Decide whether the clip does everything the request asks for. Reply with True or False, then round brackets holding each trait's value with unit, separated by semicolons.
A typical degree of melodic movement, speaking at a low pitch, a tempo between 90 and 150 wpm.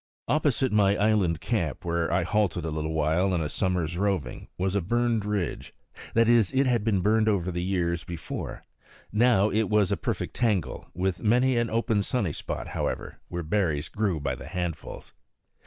False (4.2 semitones; 100 Hz; 170 wpm)